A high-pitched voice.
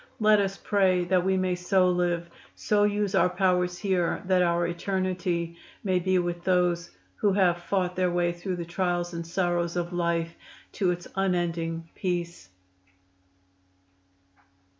No: medium, 180 Hz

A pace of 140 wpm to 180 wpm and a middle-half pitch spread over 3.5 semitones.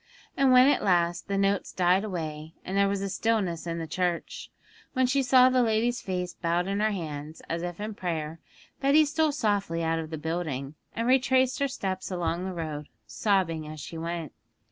No: average, 190 wpm; average, 5.2 semitones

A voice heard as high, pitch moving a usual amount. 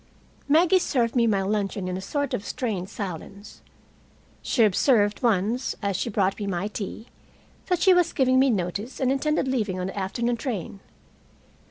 Yes: high, 215 Hz; average, 4.8 semitones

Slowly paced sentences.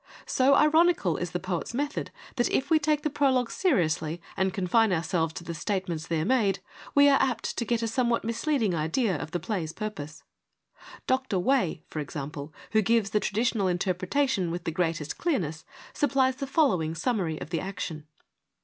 No: average, 175 wpm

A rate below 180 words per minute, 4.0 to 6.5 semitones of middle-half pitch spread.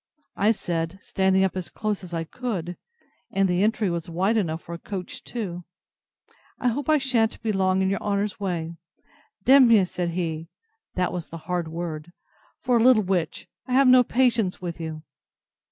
No: average, 185 wpm; average, 4.6 semitones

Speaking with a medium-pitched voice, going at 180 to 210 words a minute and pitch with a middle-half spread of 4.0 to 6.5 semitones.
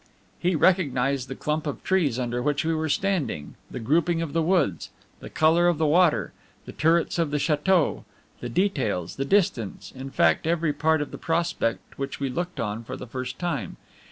Yes: medium, 150 Hz; average, 190 wpm; average, 4.7 semitones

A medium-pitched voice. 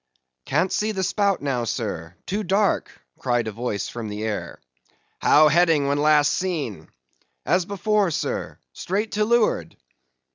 Yes: medium, 155 Hz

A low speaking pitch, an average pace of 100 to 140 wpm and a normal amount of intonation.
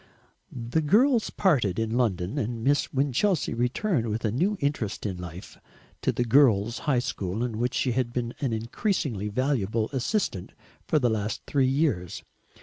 No: low, 120 Hz; average, 160 wpm; average, 4.7 semitones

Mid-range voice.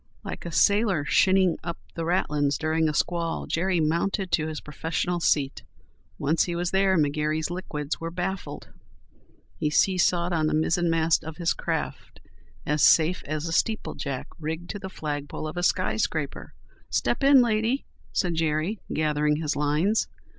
Yes: medium, 165 Hz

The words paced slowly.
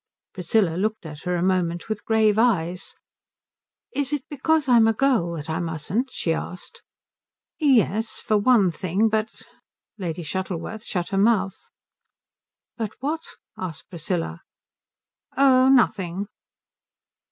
Yes: slow, 130 wpm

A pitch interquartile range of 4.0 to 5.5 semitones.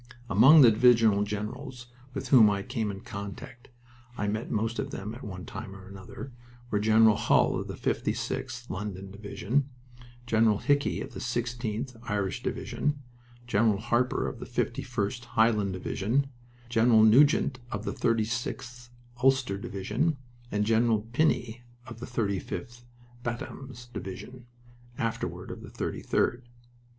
No: average, 3.0 semitones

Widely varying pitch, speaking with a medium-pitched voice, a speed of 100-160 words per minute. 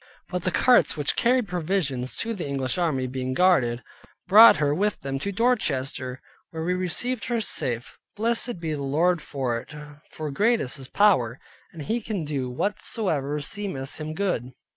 No: wide, 7.0 semitones; medium, 160 Hz; average, 170 wpm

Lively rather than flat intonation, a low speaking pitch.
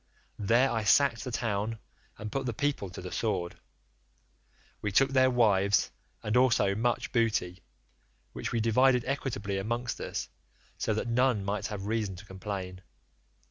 No: average, 3.7 semitones; low, 110 Hz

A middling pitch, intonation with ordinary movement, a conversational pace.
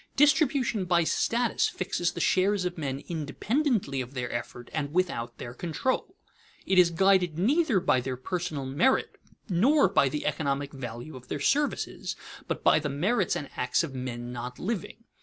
No: medium, 170 Hz; wide, 7.3 semitones; average, 170 wpm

